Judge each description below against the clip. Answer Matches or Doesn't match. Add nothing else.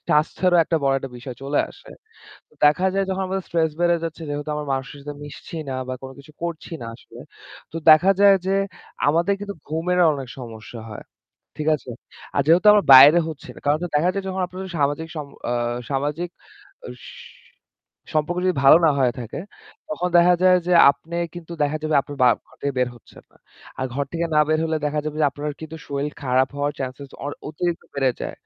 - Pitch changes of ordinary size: Matches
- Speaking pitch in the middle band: Matches